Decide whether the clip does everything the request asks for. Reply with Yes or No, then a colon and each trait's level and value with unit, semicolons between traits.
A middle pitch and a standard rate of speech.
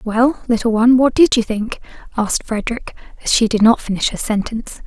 No: high, 230 Hz; average, 195 wpm